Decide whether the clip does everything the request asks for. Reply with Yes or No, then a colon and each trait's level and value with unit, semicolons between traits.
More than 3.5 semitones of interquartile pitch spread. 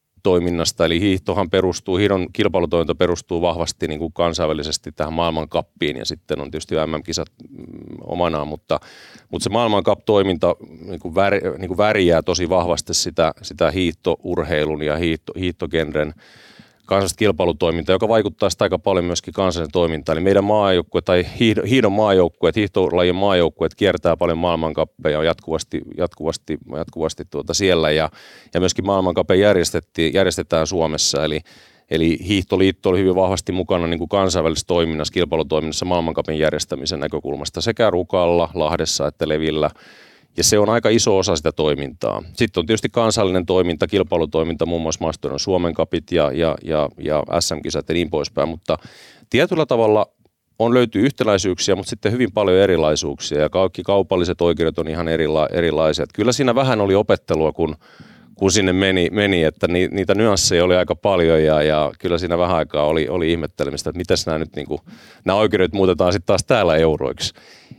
No: average, 2.9 semitones